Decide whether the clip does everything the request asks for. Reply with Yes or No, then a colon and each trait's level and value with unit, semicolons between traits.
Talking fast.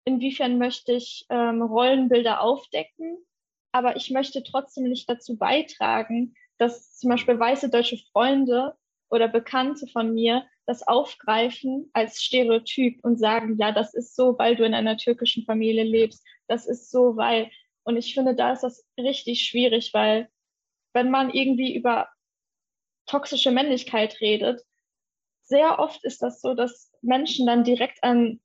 No: average, 150 wpm